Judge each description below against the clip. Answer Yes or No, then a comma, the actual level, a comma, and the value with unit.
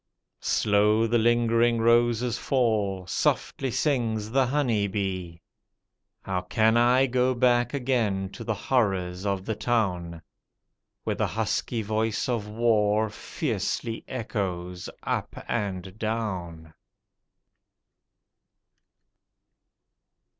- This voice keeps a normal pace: No, slow, 95 wpm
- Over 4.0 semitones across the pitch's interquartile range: No, average, 3.6 semitones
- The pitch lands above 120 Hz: No, low, 110 Hz